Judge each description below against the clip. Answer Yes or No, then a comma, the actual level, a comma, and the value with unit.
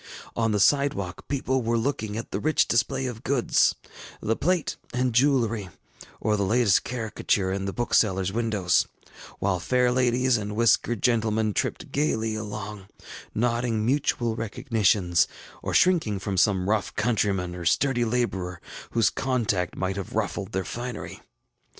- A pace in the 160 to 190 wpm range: No, average, 145 wpm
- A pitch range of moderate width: Yes, average, 3.8 semitones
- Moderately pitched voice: No, low, 110 Hz